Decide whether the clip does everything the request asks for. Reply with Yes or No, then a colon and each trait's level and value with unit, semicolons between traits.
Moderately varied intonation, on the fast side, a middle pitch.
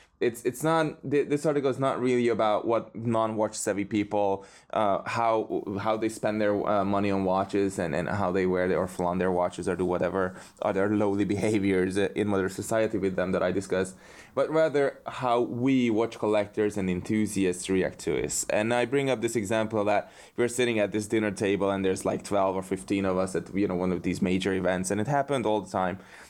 No: average, 3.1 semitones; fast, 210 wpm; low, 105 Hz